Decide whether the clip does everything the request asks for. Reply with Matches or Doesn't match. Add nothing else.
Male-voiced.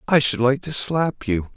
Matches